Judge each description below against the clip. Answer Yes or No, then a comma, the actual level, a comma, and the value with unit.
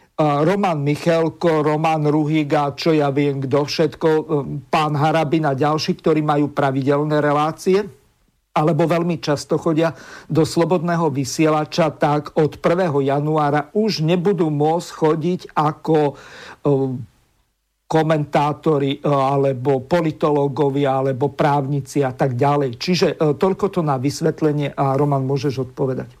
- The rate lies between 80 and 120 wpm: Yes, average, 115 wpm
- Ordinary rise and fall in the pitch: No, narrow, 2.3 semitones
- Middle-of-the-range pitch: Yes, medium, 150 Hz